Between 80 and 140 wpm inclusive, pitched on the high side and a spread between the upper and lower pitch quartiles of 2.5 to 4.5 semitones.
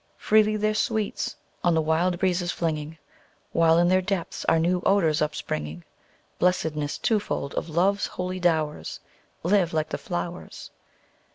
No: slow, 135 wpm; medium, 175 Hz; average, 2.9 semitones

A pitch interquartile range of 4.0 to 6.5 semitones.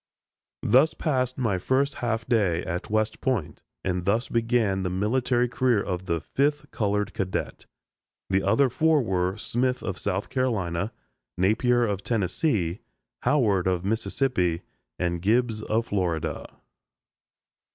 Yes: average, 5.0 semitones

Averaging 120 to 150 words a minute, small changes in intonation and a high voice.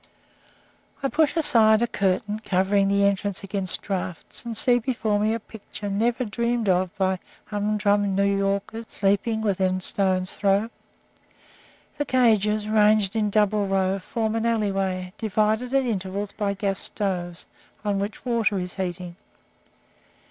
Yes: average, 140 wpm; narrow, 2.2 semitones; high, 205 Hz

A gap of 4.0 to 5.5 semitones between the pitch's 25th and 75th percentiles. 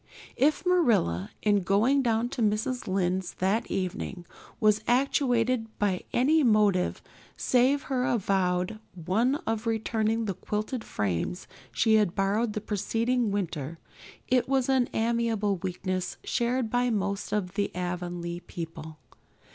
Yes: average, 4.5 semitones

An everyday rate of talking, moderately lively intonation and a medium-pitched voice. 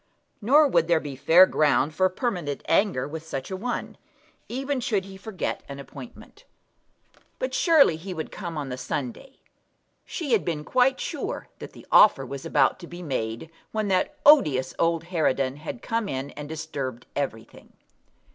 No: average, 165 wpm; wide, 7.5 semitones; medium, 165 Hz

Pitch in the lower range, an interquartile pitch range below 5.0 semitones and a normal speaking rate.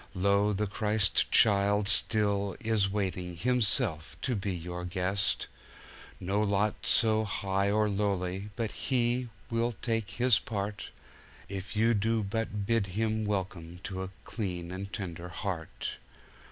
No: low, 100 Hz; narrow, 2.5 semitones; slow, 125 wpm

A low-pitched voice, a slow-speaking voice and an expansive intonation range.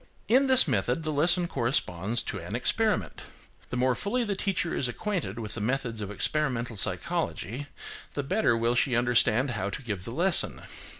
No: low, 125 Hz; average, 175 wpm; wide, 6.7 semitones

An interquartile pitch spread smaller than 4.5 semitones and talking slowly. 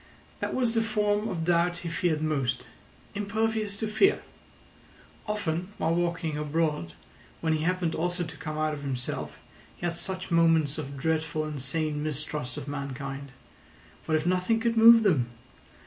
No: average, 4.0 semitones; average, 160 wpm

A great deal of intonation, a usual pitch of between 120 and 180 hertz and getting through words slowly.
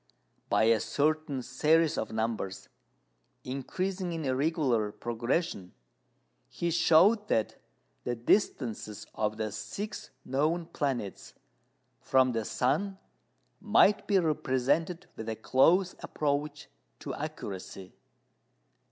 Yes: wide, 6.6 semitones; medium, 140 Hz; slow, 100 wpm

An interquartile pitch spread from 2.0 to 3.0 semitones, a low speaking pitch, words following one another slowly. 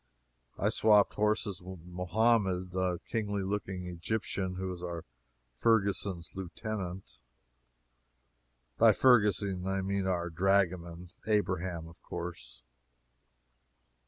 Yes: narrow, 2.5 semitones; very low, 95 Hz; slow, 100 wpm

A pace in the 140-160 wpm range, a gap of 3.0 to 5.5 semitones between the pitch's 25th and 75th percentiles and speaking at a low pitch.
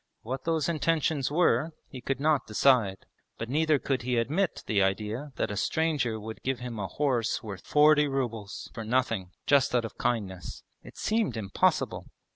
No: average, 170 wpm; average, 5.1 semitones; low, 125 Hz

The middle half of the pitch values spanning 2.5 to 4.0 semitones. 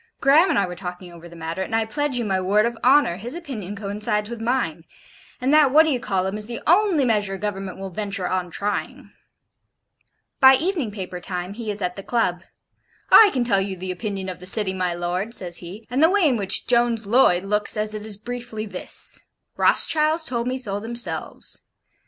No: average, 4.6 semitones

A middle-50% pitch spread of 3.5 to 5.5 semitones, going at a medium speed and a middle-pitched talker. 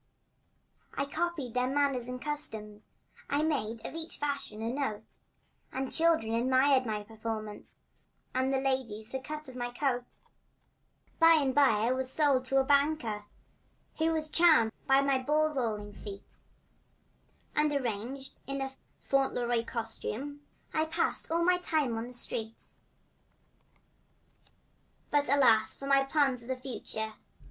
No: average, 4.0 semitones; average, 145 wpm; very high, 265 Hz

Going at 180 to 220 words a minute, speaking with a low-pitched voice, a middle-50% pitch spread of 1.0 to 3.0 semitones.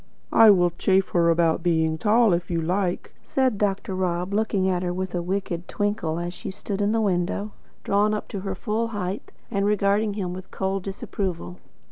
No: average, 190 wpm; high, 190 Hz; narrow, 2.6 semitones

